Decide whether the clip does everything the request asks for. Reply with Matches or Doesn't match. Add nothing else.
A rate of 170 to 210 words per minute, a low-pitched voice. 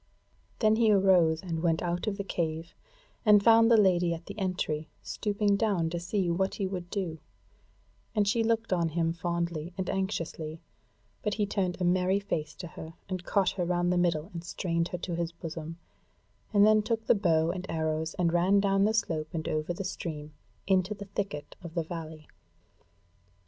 Doesn't match